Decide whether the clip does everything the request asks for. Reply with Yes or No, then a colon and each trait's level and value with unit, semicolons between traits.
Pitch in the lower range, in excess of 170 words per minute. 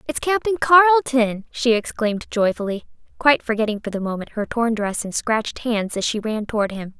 No: high, 230 Hz; average, 190 wpm